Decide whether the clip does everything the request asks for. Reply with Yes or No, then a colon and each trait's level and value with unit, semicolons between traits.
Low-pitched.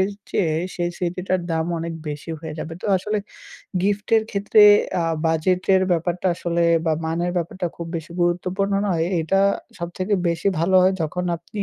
No: medium, 175 Hz